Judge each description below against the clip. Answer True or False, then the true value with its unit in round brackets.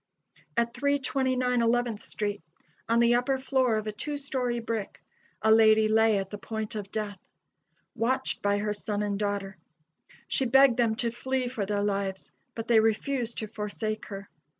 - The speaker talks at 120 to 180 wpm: True (170 wpm)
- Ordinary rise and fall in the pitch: True (3.0 semitones)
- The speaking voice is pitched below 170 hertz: False (225 Hz)